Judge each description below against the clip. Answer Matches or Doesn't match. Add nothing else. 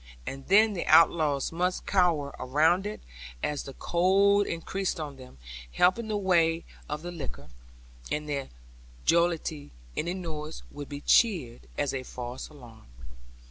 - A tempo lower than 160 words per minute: Matches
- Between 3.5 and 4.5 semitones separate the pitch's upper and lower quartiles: Matches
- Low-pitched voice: Doesn't match